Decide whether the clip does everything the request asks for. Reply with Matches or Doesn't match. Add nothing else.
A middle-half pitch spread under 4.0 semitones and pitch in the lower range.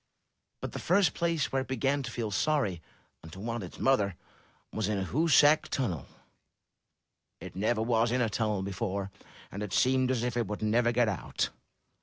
Doesn't match